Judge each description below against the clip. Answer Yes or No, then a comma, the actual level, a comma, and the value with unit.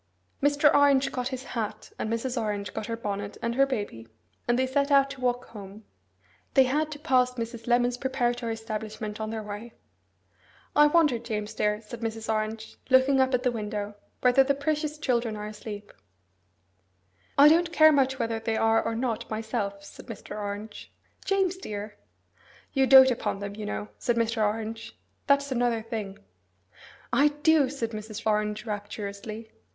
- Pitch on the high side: Yes, high, 230 Hz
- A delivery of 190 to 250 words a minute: No, average, 165 wpm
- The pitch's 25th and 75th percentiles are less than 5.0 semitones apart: Yes, average, 3.7 semitones